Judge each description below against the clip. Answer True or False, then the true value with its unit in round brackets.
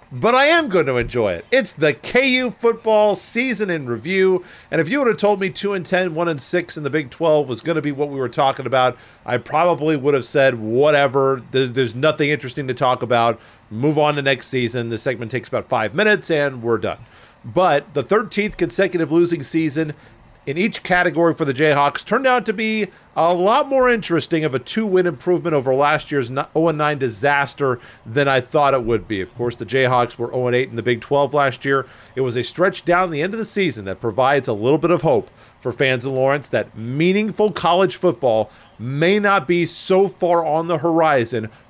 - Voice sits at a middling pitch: True (150 Hz)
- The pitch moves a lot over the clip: True (5.9 semitones)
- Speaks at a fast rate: True (215 wpm)